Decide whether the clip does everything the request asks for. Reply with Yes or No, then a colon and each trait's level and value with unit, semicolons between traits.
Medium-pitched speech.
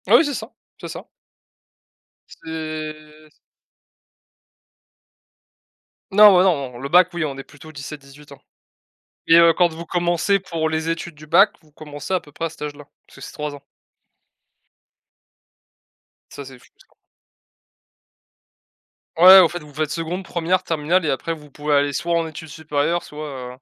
Yes: medium, 155 Hz